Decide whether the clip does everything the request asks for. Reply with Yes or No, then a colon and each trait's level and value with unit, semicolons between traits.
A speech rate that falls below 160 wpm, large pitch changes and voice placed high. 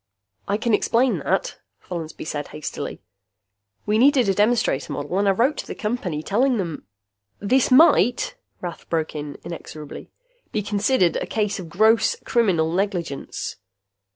Yes: average, 150 wpm; wide, 6.2 semitones; high, 200 Hz